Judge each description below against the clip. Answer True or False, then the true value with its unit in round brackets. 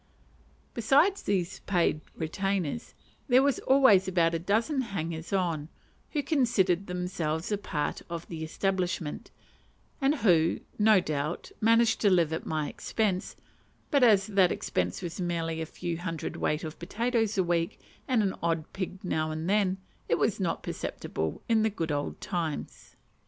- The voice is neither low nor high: True (180 Hz)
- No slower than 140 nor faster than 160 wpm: True (150 wpm)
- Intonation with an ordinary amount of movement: True (4.7 semitones)